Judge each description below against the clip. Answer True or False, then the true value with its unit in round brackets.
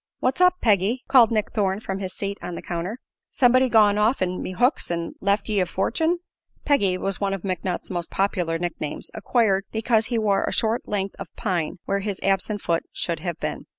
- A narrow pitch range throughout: False (3.4 semitones)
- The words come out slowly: False (200 wpm)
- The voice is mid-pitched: False (200 Hz)